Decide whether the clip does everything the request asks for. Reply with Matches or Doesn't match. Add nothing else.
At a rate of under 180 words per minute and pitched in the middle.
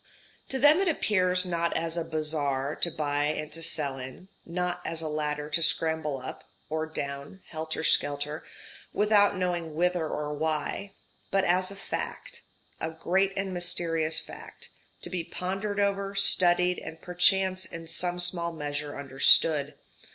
Matches